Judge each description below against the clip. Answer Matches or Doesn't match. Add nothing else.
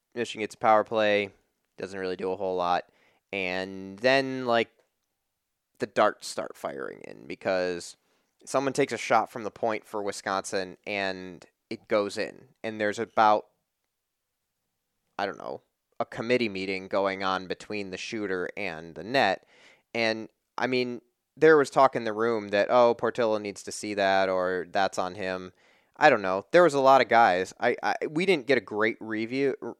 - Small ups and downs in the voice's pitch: Doesn't match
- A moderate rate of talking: Matches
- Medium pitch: Doesn't match